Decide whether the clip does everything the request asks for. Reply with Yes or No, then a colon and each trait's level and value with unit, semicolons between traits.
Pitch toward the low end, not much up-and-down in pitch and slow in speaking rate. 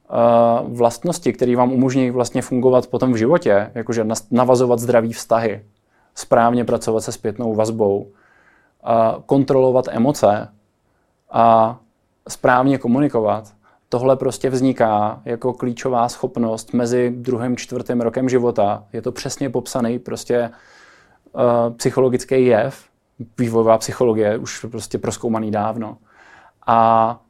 Yes: low, 120 Hz; narrow, 2.1 semitones; slow, 105 wpm